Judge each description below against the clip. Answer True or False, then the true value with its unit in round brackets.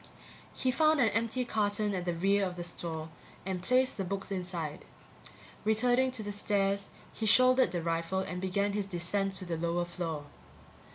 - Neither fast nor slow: True (175 wpm)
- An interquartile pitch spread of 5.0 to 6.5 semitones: False (3.7 semitones)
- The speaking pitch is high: True (195 Hz)